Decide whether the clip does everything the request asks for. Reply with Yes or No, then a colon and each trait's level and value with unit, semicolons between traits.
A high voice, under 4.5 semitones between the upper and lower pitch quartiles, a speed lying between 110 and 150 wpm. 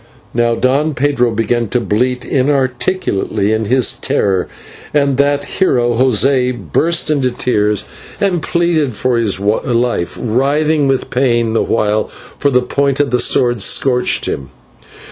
No: low, 125 Hz; average, 3.6 semitones; average, 140 wpm